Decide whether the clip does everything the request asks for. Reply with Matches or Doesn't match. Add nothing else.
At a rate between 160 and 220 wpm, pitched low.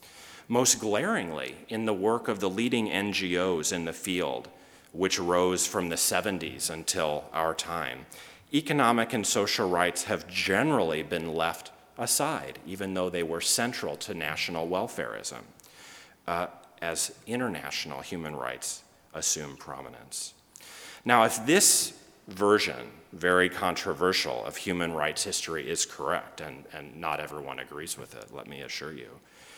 Doesn't match